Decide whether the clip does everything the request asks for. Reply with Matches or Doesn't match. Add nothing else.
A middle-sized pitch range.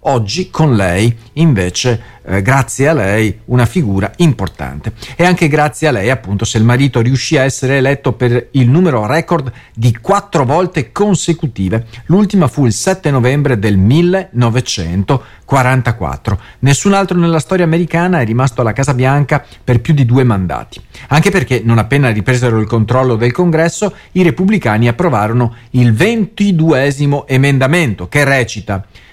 Doesn't match